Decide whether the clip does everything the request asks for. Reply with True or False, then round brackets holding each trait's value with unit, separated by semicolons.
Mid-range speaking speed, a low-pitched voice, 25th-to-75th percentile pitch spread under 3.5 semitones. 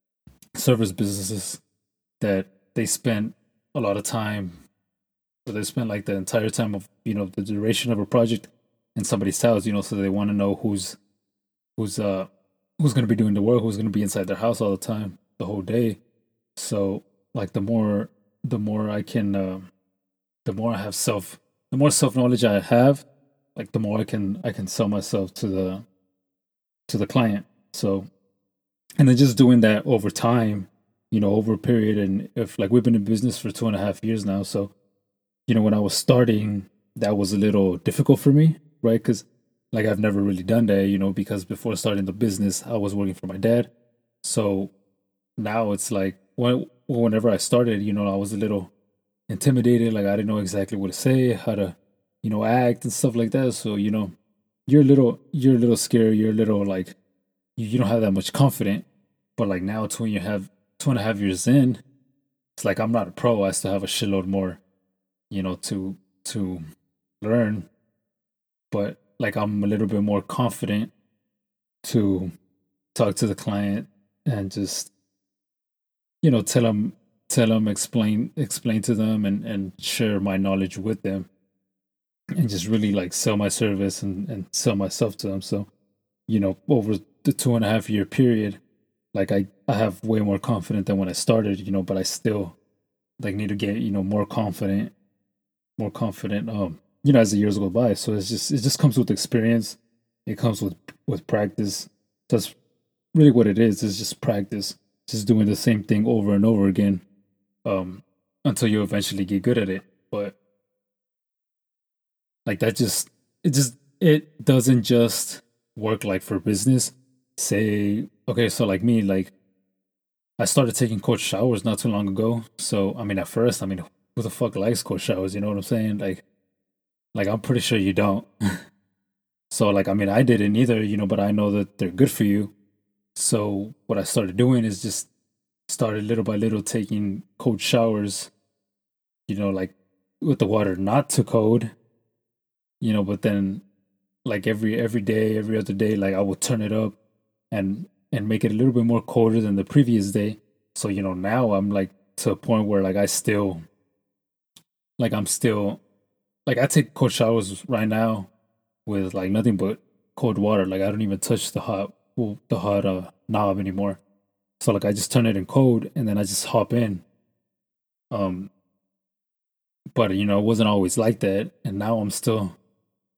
True (190 wpm; 105 Hz; 2.8 semitones)